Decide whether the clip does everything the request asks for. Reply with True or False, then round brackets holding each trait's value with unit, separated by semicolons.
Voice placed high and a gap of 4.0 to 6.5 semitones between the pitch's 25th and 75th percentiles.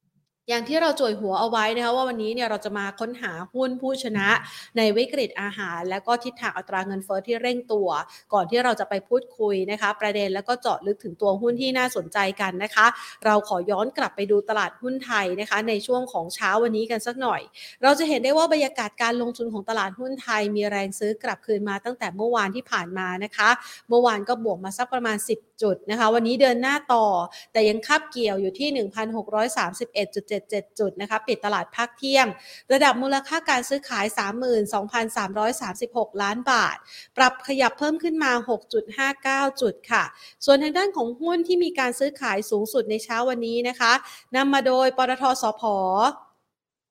False (230 Hz; 3.6 semitones)